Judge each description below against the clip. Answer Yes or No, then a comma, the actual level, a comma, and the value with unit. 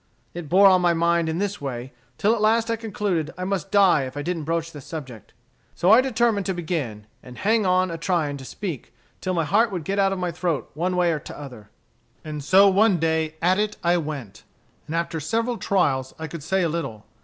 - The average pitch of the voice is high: No, medium, 170 Hz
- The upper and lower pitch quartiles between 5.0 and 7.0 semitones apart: No, average, 4.5 semitones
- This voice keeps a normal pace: No, fast, 225 wpm